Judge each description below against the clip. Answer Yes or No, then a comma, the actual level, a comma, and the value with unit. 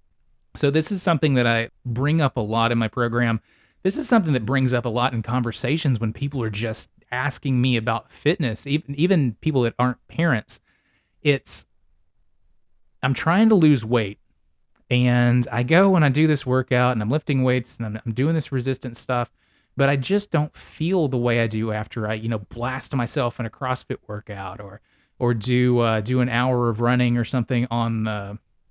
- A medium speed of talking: Yes, average, 195 wpm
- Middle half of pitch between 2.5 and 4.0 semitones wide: Yes, average, 3.4 semitones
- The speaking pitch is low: Yes, low, 125 Hz